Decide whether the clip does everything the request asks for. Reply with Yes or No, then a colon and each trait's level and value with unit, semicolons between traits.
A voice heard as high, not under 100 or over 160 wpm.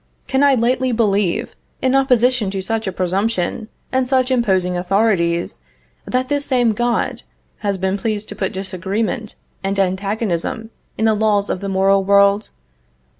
Yes: high, 210 Hz; average, 150 wpm